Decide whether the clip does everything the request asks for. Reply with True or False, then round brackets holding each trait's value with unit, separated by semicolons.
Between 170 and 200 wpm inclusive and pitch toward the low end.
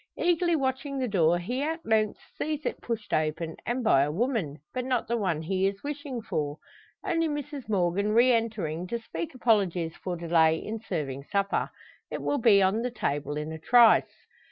False (185 wpm; 215 Hz)